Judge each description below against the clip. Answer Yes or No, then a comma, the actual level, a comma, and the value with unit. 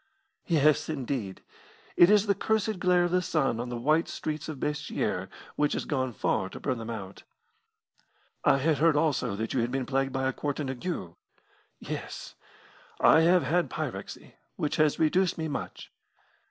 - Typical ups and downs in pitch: Yes, average, 4.2 semitones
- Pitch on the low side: No, medium, 150 Hz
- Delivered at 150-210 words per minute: Yes, average, 175 wpm